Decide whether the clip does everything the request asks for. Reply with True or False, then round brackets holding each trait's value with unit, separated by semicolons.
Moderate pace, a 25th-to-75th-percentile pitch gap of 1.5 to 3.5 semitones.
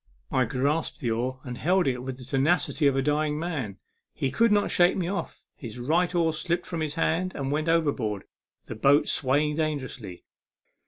False (190 wpm; 4.3 semitones)